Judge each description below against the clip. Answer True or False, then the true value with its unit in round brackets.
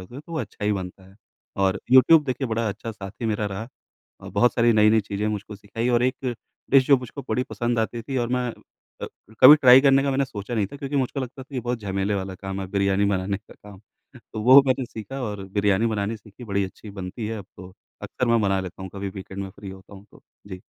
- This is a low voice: True (110 Hz)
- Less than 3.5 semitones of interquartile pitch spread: False (4.2 semitones)